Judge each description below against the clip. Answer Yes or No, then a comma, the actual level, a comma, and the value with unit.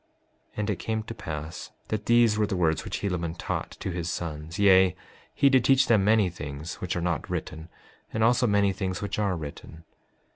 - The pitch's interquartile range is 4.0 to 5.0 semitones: Yes, average, 4.5 semitones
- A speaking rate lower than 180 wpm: No, fast, 205 wpm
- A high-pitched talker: No, very low, 95 Hz